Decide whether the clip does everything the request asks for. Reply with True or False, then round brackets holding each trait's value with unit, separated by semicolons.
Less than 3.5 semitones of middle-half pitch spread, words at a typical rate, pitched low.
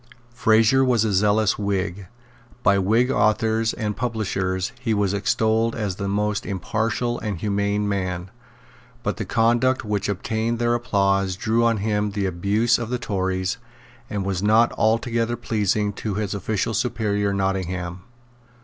True (2.5 semitones; 145 wpm; 105 Hz)